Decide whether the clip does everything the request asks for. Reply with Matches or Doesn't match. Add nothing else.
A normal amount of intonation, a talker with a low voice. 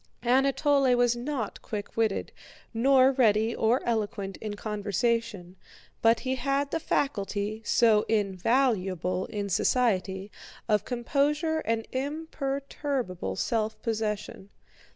Doesn't match